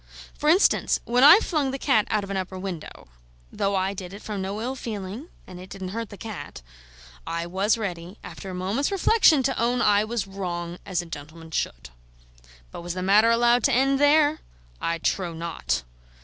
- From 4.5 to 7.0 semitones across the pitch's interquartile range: Yes, average, 5.1 semitones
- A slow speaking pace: No, average, 195 wpm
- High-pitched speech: Yes, high, 200 Hz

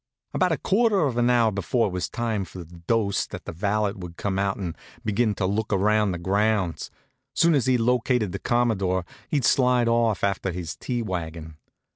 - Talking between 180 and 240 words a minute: Yes, average, 190 wpm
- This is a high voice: No, low, 105 Hz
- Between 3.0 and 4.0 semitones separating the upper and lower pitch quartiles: No, average, 4.4 semitones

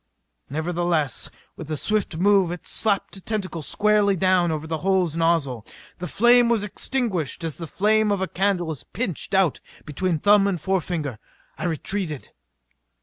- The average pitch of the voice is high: No, medium, 180 Hz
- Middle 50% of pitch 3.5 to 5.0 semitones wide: Yes, average, 4.0 semitones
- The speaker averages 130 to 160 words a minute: Yes, average, 155 wpm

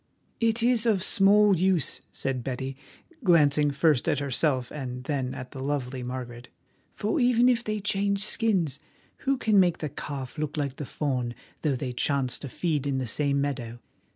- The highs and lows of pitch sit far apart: Yes, wide, 7.1 semitones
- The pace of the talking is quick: No, average, 175 wpm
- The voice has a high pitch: No, medium, 145 Hz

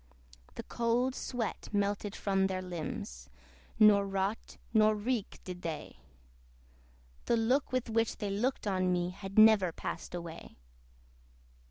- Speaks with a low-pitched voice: No, high, 205 Hz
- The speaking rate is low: Yes, slow, 130 wpm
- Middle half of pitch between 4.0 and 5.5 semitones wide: No, average, 3.2 semitones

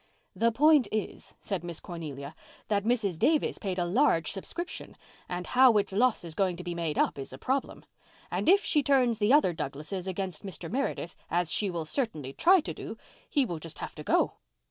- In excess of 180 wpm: Yes, average, 200 wpm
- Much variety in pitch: Yes, wide, 6.9 semitones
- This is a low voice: No, high, 195 Hz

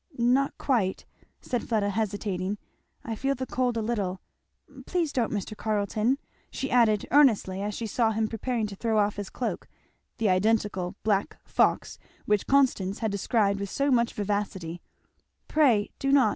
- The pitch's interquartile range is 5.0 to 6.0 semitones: No, average, 3.3 semitones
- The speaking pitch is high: Yes, high, 220 Hz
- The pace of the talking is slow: No, average, 160 wpm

